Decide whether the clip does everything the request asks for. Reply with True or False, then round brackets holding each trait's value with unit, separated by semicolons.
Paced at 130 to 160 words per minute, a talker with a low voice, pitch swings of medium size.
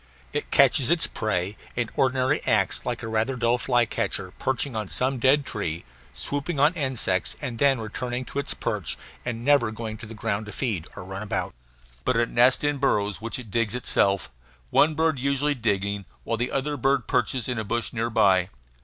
False (190 wpm; 120 Hz; 3.9 semitones)